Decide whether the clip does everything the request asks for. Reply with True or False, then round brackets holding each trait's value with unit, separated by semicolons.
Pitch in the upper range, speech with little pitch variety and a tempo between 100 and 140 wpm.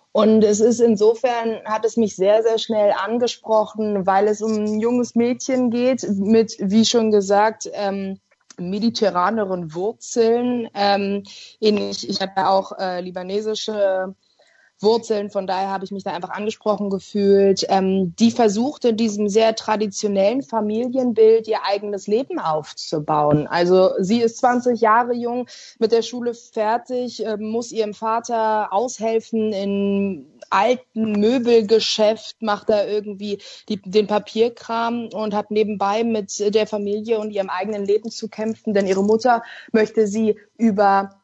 True (215 Hz; 2.3 semitones; 135 wpm)